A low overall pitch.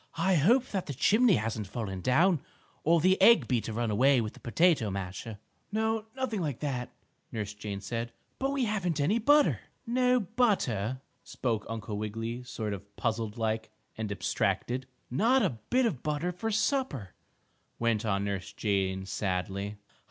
Yes: low, 125 Hz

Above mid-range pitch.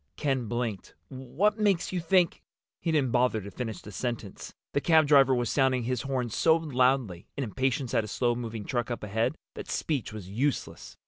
No: low, 125 Hz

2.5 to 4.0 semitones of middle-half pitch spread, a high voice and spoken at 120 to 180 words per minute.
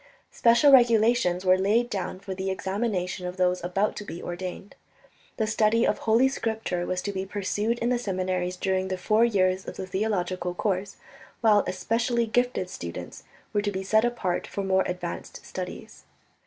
Yes: average, 3.4 semitones; high, 195 Hz; average, 170 wpm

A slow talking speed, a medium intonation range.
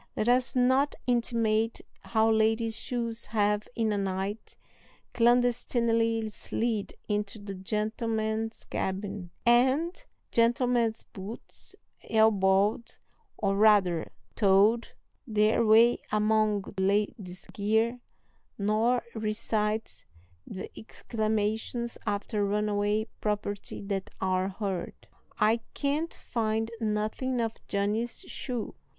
No: slow, 95 wpm; narrow, 2.1 semitones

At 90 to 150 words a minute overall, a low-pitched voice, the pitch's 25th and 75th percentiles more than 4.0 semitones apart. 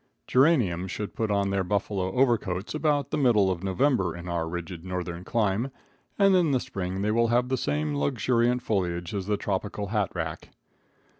No: average, 175 wpm; low, 100 Hz; average, 5.1 semitones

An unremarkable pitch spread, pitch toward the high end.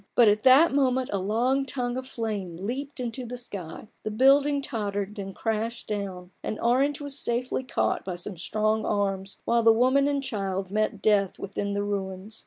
Yes: average, 4.3 semitones; high, 220 Hz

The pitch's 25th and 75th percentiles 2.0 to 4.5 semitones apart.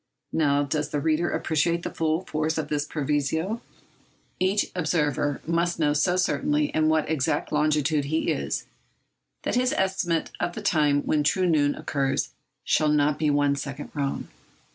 Yes: average, 2.7 semitones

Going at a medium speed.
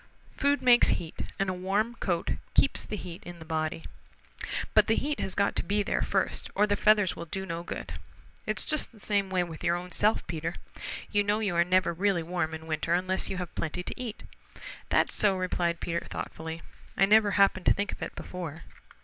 No: fast, 210 wpm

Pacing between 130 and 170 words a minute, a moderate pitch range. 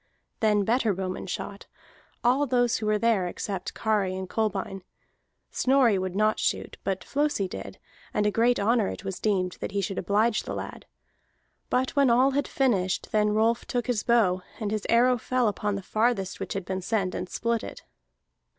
No: average, 185 wpm; average, 3.5 semitones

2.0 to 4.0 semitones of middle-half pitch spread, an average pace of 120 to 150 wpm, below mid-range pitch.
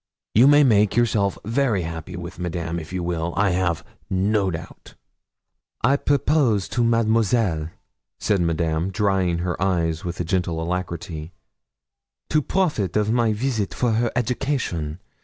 No: average, 5.2 semitones; average, 140 wpm; very low, 95 Hz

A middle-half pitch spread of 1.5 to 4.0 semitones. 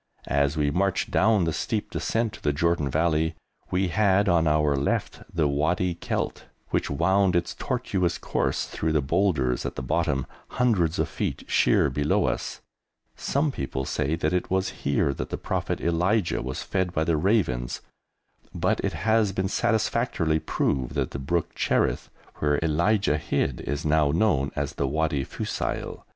No: average, 4.8 semitones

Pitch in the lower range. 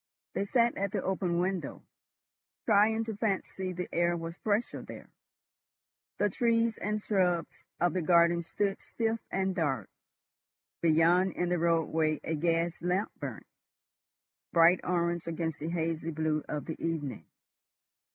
No: medium, 175 Hz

